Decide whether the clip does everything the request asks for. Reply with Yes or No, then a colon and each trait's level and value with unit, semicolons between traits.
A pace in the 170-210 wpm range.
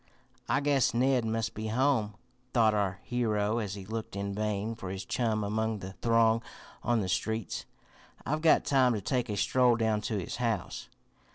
Yes: average, 180 wpm